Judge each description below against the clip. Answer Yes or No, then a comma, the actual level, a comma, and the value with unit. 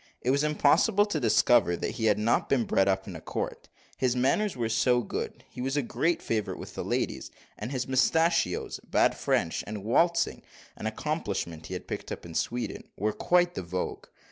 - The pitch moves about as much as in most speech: No, wide, 6.3 semitones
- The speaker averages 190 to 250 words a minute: Yes, average, 195 wpm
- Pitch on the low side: Yes, low, 120 Hz